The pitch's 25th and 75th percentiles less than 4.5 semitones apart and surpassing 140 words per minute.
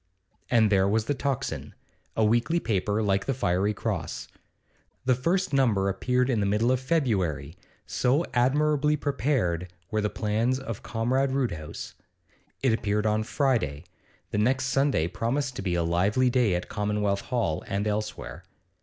No: average, 4.8 semitones; average, 155 wpm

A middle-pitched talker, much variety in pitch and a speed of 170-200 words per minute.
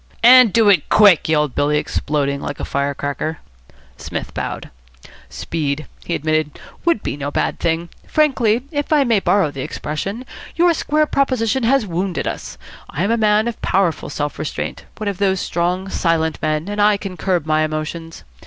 Yes: medium, 180 Hz; wide, 6.1 semitones; average, 175 wpm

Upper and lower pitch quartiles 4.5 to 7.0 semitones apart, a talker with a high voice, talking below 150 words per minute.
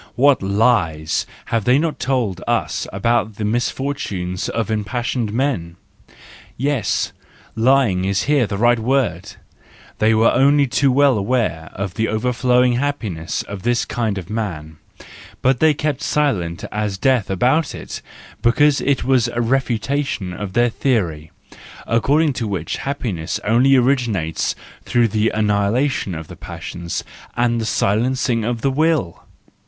No: average, 4.9 semitones; low, 115 Hz; average, 140 wpm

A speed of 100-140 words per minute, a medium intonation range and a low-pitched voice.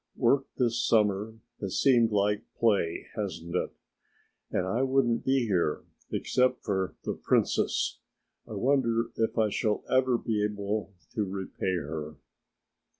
Yes: slow, 135 wpm; average, 3.4 semitones; low, 110 Hz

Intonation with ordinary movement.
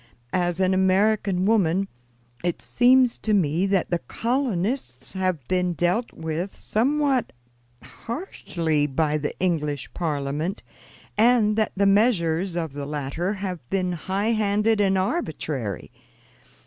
Yes: average, 4.8 semitones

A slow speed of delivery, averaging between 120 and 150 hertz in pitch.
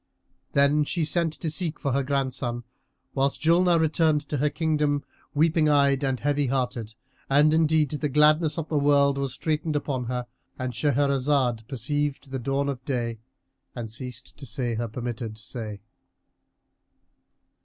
No: average, 145 wpm; medium, 140 Hz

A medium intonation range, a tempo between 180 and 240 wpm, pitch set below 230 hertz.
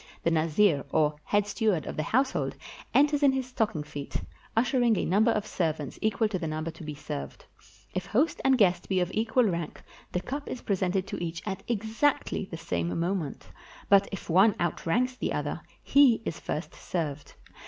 No: wide, 5.7 semitones; average, 185 wpm; high, 190 Hz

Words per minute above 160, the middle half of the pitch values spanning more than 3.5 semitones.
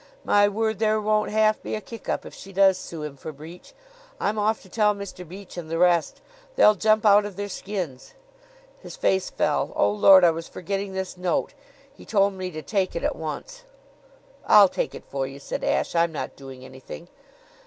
Yes: fast, 205 wpm; average, 4.1 semitones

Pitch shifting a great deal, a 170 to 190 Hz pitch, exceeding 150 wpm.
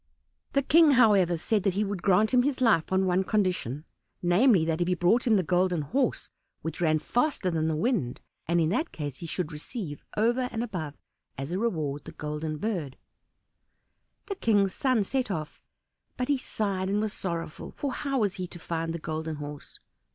Yes: wide, 5.9 semitones; medium, 185 Hz; average, 190 wpm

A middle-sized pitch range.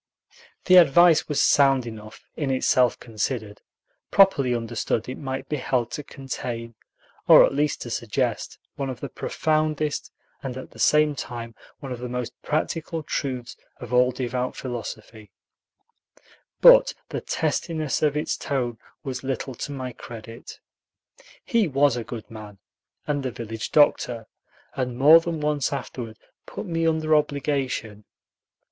Yes: average, 3.9 semitones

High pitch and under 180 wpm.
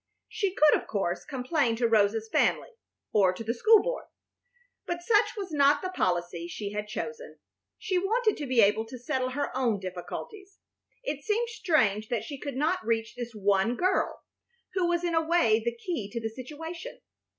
No: very high, 260 Hz; average, 185 wpm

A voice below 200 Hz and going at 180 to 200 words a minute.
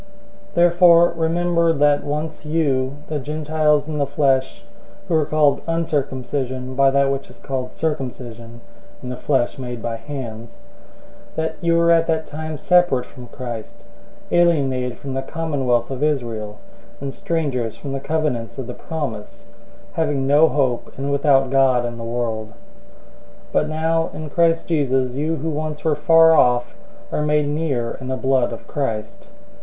No: medium, 140 Hz; average, 160 wpm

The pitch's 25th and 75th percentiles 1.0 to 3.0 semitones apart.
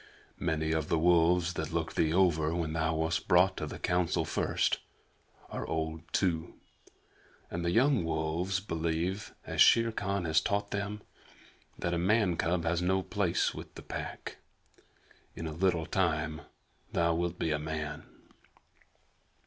Yes: narrow, 2.6 semitones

